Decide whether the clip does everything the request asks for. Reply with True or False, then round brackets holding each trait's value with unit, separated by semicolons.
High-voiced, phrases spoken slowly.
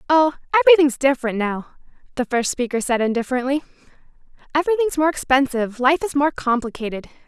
True (270 Hz; 130 wpm)